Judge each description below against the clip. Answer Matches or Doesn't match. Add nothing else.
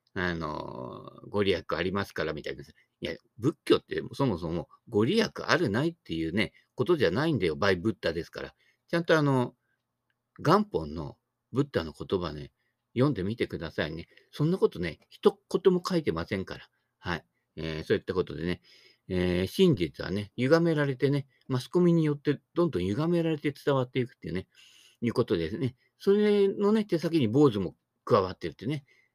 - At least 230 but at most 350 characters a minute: Doesn't match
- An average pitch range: Doesn't match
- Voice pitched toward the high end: Doesn't match